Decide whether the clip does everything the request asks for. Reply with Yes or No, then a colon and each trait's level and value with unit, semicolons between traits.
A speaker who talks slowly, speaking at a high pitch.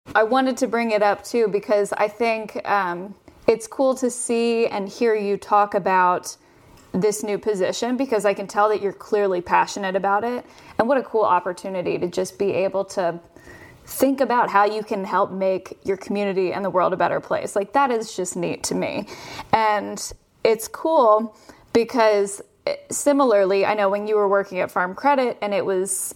No: average, 190 wpm; high, 205 Hz